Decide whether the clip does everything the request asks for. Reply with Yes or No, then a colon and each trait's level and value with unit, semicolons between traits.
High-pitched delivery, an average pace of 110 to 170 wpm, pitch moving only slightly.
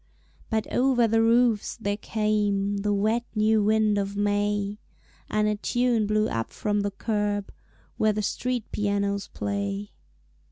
Yes: high, 210 Hz; average, 145 wpm; narrow, 1.3 semitones